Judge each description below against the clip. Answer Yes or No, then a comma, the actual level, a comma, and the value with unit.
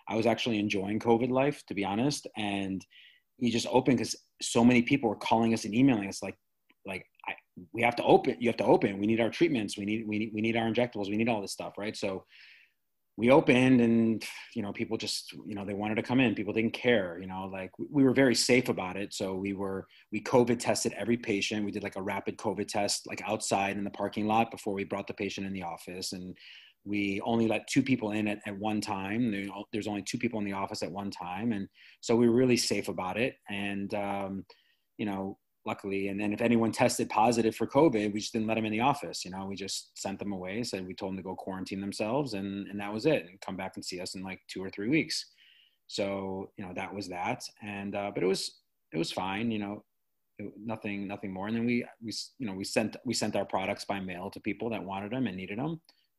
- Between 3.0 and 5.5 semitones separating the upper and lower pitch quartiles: No, narrow, 2.6 semitones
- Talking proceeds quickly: Yes, fast, 250 wpm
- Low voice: Yes, low, 105 Hz